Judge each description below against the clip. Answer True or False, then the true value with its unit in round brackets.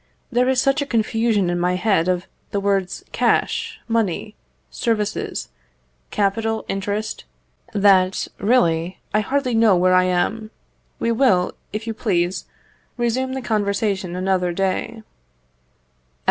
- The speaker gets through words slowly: True (125 wpm)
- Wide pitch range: False (3.7 semitones)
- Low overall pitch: False (205 Hz)